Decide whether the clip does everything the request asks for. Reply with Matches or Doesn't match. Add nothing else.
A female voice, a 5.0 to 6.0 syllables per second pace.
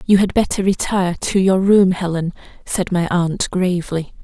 Doesn't match